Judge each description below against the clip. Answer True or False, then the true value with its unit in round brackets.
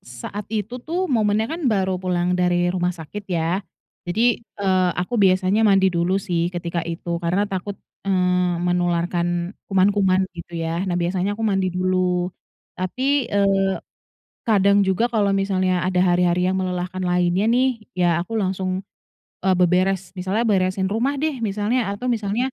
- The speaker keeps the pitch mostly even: True (2.3 semitones)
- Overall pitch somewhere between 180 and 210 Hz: True (185 Hz)